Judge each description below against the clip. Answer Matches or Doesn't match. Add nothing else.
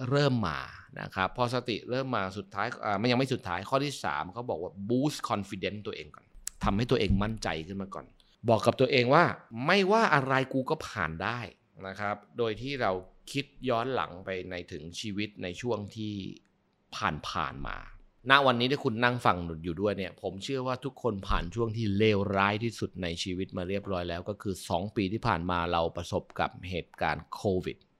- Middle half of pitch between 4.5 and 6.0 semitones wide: Matches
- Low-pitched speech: Matches